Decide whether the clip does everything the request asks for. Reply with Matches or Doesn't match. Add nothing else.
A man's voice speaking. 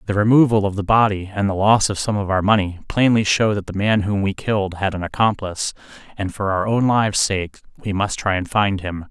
Matches